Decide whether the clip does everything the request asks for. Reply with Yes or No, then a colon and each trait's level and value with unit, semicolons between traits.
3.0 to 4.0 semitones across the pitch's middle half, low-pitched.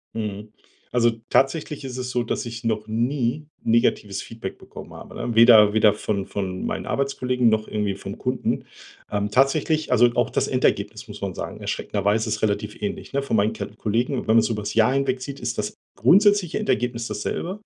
Yes: average, 3.4 semitones; low, 115 Hz